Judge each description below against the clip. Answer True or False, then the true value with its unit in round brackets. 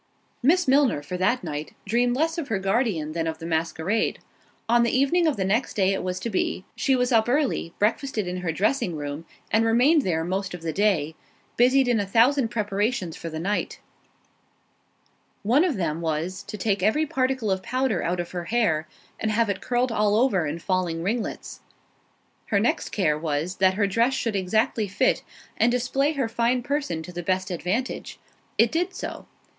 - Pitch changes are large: True (5.7 semitones)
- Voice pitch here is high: True (210 Hz)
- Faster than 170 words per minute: True (185 wpm)